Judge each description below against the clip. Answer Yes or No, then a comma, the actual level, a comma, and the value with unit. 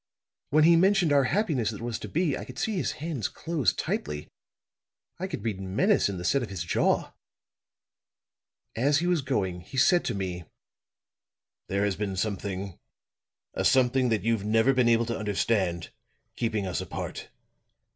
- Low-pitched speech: Yes, low, 115 Hz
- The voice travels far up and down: Yes, wide, 6.7 semitones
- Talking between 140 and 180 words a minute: Yes, average, 165 wpm